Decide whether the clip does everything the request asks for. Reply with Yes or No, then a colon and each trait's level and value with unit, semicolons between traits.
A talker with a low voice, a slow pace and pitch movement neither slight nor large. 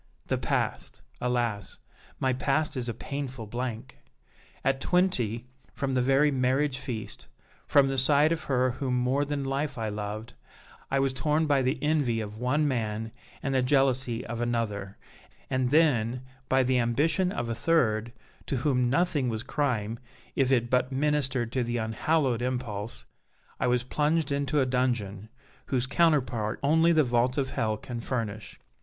No: low, 130 Hz; average, 160 wpm; average, 3.2 semitones